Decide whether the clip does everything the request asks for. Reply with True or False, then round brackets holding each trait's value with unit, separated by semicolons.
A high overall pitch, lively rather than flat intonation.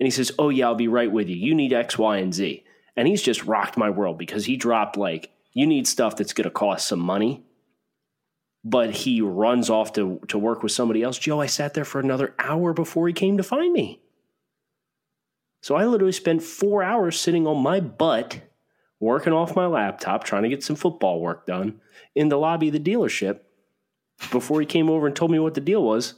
False (150 Hz; 5.9 semitones)